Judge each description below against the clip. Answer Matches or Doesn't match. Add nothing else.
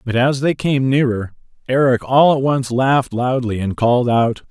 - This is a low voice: Matches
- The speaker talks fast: Doesn't match